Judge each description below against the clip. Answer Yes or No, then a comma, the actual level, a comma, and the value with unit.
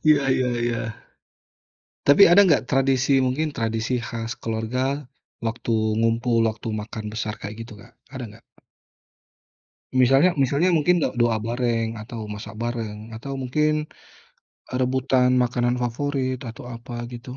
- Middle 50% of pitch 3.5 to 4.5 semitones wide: No, average, 2.9 semitones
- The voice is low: Yes, low, 125 Hz